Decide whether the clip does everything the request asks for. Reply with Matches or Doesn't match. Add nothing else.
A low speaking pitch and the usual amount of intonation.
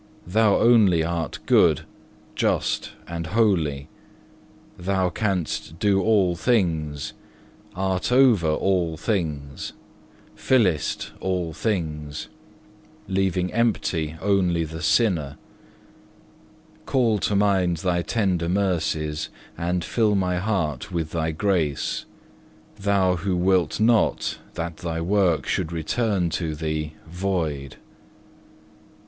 Matches